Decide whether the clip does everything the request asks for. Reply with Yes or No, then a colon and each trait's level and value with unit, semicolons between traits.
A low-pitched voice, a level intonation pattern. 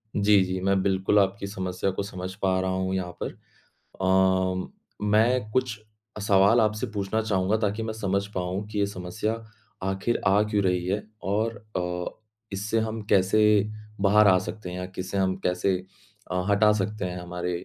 Yes: very low, 95 Hz; narrow, 2.2 semitones